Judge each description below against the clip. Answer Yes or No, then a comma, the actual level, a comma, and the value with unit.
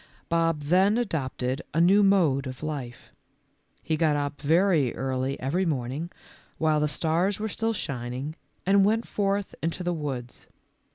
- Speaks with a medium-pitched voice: Yes, medium, 160 Hz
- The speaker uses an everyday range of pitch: No, wide, 5.7 semitones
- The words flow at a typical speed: Yes, average, 150 wpm